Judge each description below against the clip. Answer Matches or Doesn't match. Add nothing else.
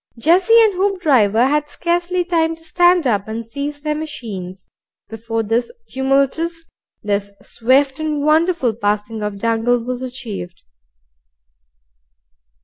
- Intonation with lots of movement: Matches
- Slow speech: Matches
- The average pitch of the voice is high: Matches